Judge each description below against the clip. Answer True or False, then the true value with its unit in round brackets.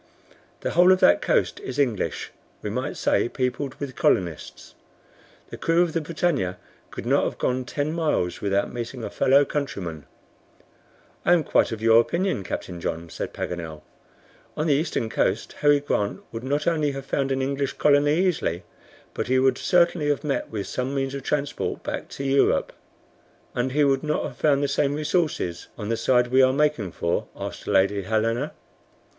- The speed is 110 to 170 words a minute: False (180 wpm)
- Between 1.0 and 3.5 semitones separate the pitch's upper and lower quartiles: False (4.8 semitones)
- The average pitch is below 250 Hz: True (135 Hz)